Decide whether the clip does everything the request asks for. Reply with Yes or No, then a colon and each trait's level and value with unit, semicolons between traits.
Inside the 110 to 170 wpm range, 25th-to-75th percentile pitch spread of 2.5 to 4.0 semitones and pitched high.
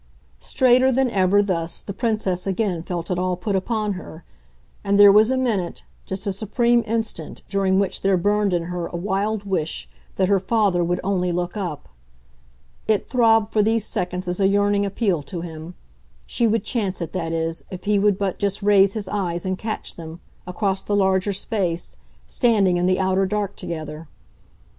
No: average, 185 wpm; average, 2.8 semitones; high, 195 Hz